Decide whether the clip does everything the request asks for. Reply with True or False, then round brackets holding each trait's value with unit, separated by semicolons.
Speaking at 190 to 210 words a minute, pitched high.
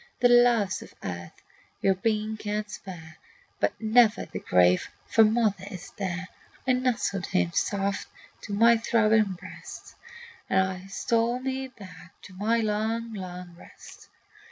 False (135 wpm; 210 Hz)